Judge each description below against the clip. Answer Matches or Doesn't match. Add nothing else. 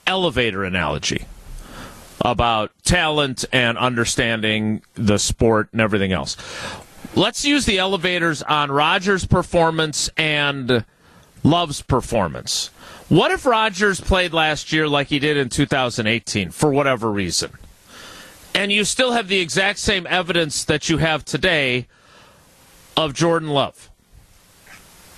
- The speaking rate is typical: Doesn't match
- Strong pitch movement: Matches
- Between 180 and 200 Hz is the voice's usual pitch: Doesn't match